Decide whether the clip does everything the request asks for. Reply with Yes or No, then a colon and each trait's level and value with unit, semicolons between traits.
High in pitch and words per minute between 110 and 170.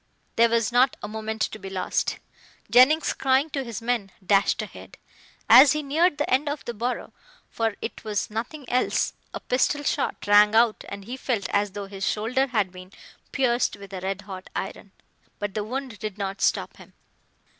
No: high, 225 Hz; average, 190 wpm